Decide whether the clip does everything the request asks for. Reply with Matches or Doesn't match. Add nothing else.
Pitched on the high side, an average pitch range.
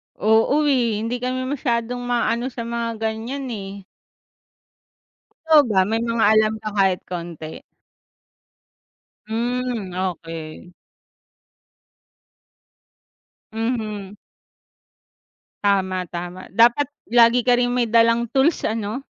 Matches